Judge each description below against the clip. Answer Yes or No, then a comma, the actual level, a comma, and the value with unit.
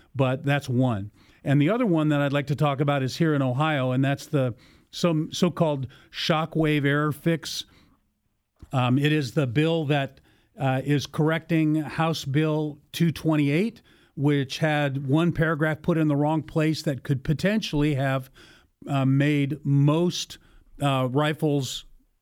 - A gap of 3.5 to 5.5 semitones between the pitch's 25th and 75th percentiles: No, narrow, 2.4 semitones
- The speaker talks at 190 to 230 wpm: No, average, 150 wpm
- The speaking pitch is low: No, medium, 150 Hz